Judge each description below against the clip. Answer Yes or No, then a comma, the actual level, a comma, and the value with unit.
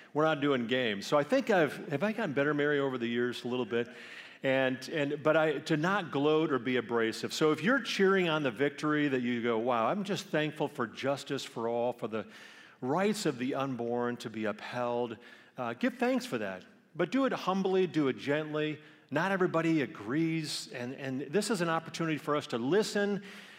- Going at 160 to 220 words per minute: Yes, fast, 205 wpm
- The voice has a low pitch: No, medium, 150 Hz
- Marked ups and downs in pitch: Yes, wide, 5.9 semitones